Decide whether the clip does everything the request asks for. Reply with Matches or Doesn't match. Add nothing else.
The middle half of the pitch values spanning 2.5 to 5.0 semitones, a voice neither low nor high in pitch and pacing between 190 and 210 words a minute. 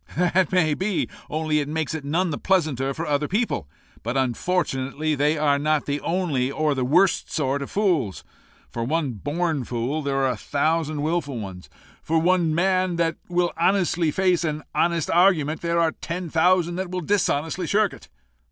Doesn't match